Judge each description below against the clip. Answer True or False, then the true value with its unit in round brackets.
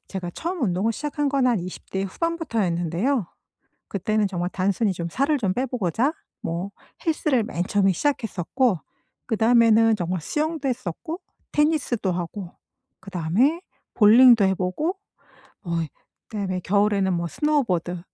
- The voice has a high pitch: True (210 Hz)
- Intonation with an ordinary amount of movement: False (6.4 semitones)